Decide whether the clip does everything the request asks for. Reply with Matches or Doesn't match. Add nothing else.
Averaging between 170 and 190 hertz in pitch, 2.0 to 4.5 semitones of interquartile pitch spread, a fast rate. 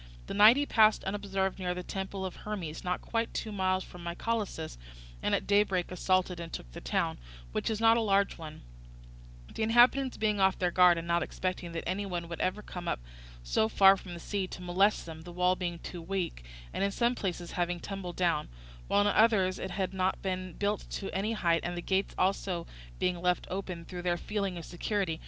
Matches